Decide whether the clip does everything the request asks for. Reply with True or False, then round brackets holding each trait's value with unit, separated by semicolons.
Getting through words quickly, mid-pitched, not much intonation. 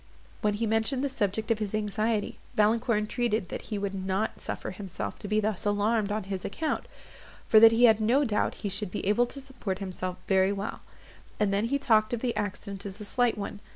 False (215 wpm; 210 Hz; 2.3 semitones)